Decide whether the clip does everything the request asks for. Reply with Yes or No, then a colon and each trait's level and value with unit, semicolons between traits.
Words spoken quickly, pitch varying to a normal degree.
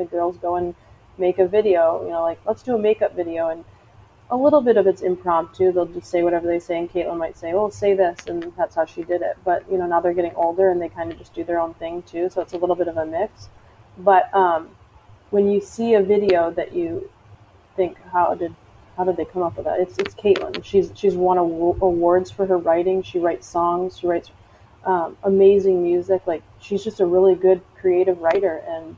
No: fast, 235 wpm; narrow, 2.2 semitones